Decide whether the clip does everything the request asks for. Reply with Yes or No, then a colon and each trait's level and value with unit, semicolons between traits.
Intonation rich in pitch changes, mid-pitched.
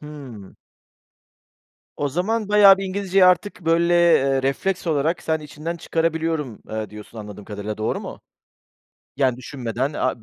Yes: wide, 6.2 semitones; medium, 150 Hz